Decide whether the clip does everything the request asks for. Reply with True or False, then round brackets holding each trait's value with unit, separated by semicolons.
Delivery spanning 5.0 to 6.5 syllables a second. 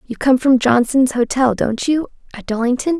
False (4.8 syllables/s)